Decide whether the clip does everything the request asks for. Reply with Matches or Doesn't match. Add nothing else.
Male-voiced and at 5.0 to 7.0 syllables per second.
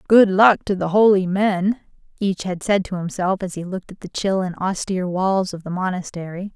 Doesn't match